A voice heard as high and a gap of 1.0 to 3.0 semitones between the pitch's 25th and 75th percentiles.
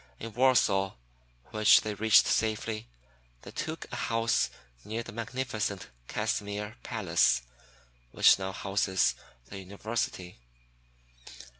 No: low, 105 Hz; average, 2.7 semitones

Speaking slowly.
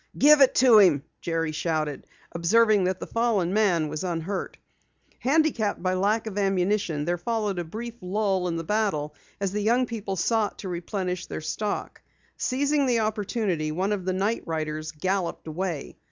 No: average, 170 wpm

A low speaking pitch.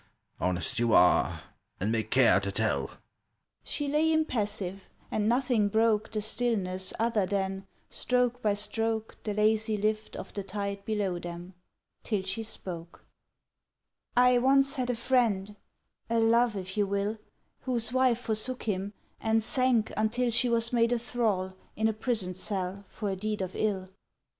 No: high, 215 Hz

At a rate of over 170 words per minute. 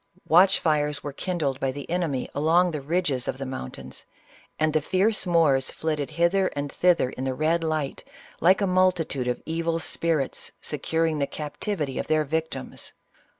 No: average, 165 wpm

